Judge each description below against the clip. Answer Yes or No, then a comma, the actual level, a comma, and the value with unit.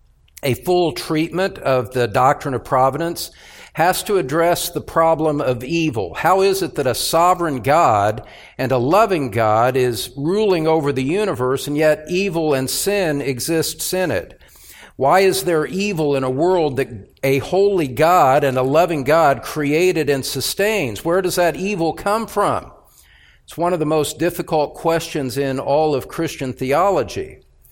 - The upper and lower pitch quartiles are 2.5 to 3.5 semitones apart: No, average, 4.7 semitones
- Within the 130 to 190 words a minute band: Yes, average, 160 wpm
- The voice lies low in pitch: No, medium, 155 Hz